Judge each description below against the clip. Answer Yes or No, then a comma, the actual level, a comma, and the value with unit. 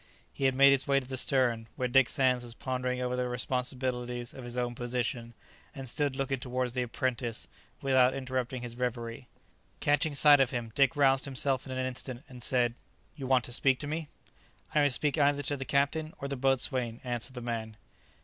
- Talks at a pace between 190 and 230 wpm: Yes, average, 200 wpm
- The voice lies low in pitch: Yes, low, 130 Hz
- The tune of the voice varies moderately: No, narrow, 1.8 semitones